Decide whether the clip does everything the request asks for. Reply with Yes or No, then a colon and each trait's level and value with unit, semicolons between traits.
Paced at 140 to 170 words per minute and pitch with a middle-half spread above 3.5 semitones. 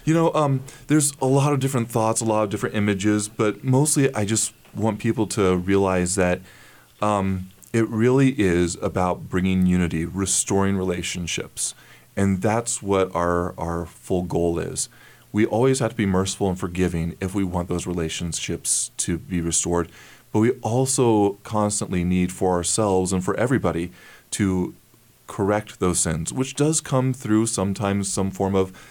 Yes: average, 160 wpm; average, 4.0 semitones